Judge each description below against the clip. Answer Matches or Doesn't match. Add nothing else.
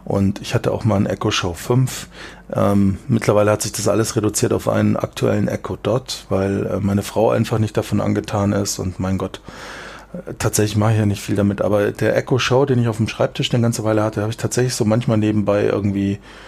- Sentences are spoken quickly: Matches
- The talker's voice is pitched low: Matches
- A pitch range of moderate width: Doesn't match